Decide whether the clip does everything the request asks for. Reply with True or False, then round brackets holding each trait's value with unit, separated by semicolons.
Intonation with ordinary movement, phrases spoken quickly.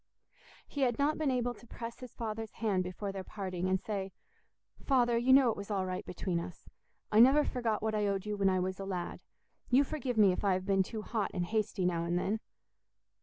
True (4.2 semitones; 225 wpm)